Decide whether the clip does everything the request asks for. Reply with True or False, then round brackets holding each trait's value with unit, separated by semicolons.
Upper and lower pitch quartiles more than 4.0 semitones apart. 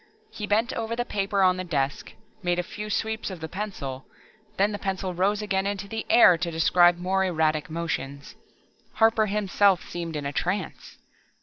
False (3.6 semitones)